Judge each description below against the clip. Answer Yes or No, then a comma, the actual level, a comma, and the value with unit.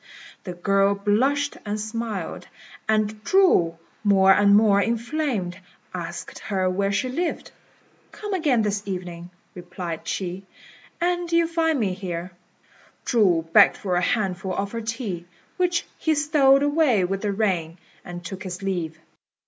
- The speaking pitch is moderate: No, high, 200 Hz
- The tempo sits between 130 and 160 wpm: Yes, average, 140 wpm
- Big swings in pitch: Yes, wide, 5.8 semitones